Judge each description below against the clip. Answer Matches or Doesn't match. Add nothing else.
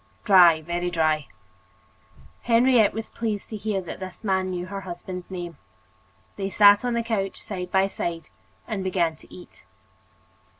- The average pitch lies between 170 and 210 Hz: Matches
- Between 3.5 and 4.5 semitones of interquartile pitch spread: Doesn't match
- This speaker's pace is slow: Doesn't match